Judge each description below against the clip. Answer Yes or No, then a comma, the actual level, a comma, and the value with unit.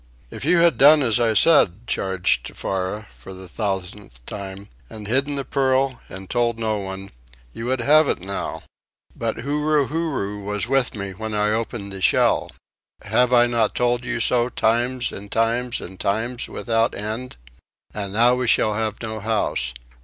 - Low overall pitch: Yes, low, 115 Hz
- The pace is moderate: Yes, average, 170 wpm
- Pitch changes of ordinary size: Yes, average, 3.8 semitones